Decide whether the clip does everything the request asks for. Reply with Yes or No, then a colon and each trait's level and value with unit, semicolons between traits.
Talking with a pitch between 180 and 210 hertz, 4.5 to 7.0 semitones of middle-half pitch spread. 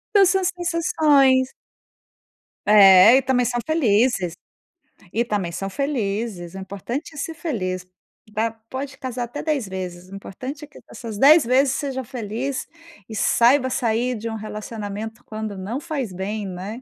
No: high, 235 Hz; average, 5.0 semitones